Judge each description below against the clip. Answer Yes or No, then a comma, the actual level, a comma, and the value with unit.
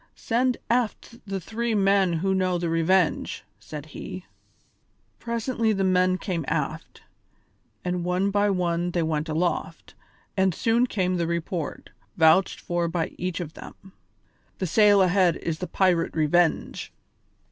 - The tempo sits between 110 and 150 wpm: Yes, average, 140 wpm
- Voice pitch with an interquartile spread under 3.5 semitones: Yes, average, 2.7 semitones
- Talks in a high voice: No, medium, 180 Hz